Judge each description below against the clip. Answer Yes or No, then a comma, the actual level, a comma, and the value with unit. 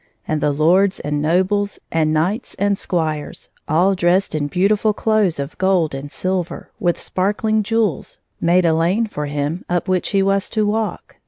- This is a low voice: No, medium, 185 Hz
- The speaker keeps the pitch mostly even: No, average, 4.3 semitones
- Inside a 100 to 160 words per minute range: No, average, 170 wpm